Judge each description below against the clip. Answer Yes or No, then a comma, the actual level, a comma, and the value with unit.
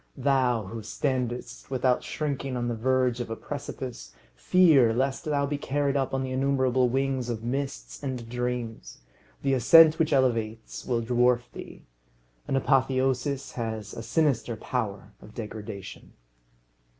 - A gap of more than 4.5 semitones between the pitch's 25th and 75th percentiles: No, average, 2.9 semitones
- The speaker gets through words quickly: No, average, 140 wpm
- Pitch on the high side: No, low, 125 Hz